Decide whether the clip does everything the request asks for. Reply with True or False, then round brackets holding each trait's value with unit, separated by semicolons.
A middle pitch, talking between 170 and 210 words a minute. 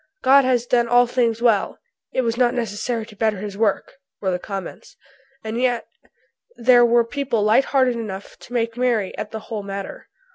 False (230 Hz; 185 wpm)